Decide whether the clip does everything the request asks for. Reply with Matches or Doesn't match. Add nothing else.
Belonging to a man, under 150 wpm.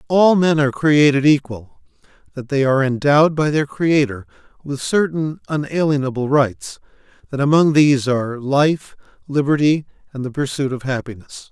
Matches